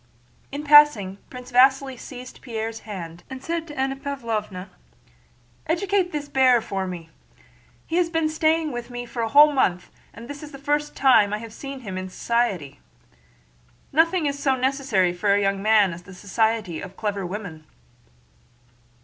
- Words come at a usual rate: Yes, average, 165 wpm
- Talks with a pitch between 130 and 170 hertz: No, high, 245 Hz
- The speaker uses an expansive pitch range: Yes, wide, 6.2 semitones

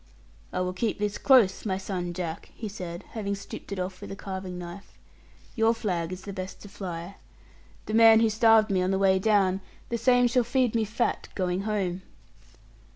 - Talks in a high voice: Yes, high, 195 Hz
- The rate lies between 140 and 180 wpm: No, average, 195 wpm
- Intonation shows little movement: No, average, 3.2 semitones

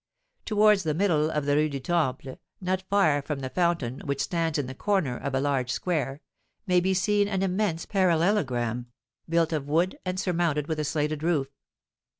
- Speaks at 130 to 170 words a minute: No, average, 180 wpm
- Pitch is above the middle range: No, medium, 160 Hz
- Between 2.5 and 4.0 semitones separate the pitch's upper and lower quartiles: No, average, 4.6 semitones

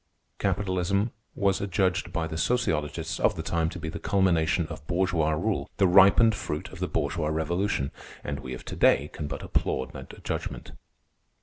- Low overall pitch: Yes, very low, 85 Hz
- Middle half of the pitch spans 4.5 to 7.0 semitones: No, average, 3.5 semitones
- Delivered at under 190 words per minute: Yes, average, 175 wpm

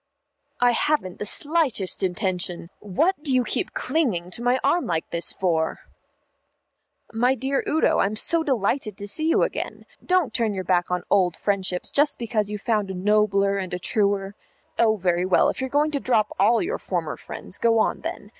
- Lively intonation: Yes, wide, 5.9 semitones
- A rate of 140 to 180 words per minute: No, average, 190 wpm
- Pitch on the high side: Yes, high, 210 Hz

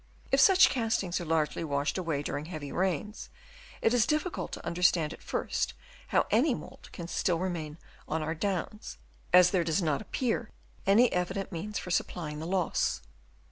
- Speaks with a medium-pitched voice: Yes, medium, 180 Hz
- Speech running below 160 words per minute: No, average, 170 wpm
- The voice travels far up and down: No, average, 4.6 semitones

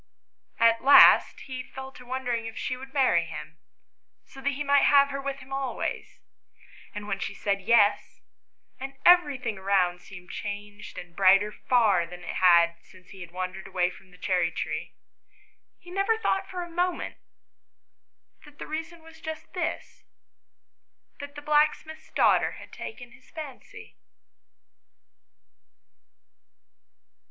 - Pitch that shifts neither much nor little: No, wide, 7.1 semitones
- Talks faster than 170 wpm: No, average, 145 wpm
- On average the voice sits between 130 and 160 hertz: No, high, 245 Hz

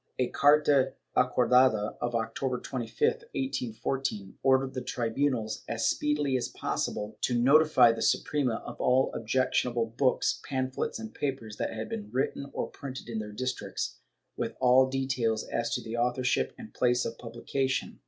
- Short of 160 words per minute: Yes, average, 150 wpm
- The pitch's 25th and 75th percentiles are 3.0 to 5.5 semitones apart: No, narrow, 2.6 semitones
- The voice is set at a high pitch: No, low, 125 Hz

